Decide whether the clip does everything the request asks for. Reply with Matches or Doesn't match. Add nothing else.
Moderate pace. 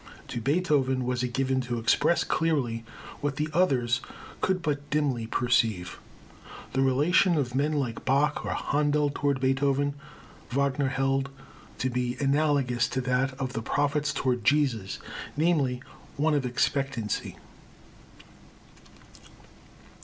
Doesn't match